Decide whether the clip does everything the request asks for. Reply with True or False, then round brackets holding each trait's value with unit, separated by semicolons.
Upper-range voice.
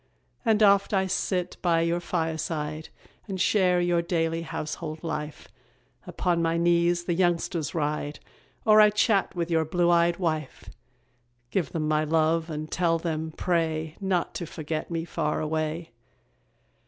False (165 Hz)